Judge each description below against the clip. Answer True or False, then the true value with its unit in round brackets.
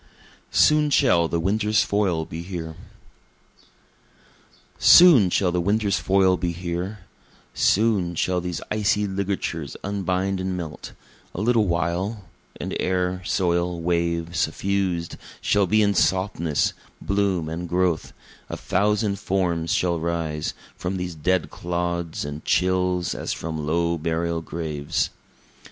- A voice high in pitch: False (90 Hz)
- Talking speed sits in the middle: False (125 wpm)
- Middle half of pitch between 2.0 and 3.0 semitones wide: True (2.7 semitones)